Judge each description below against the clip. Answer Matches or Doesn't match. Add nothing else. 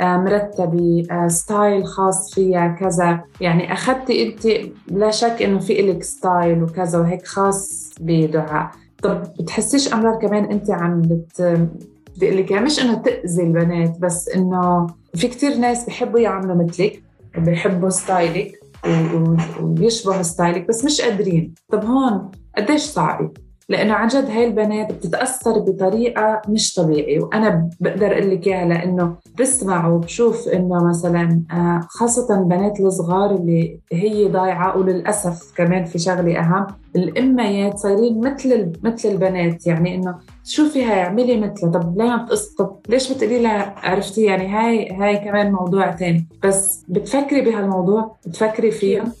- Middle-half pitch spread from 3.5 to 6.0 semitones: Matches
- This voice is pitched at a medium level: Doesn't match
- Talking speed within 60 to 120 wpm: Doesn't match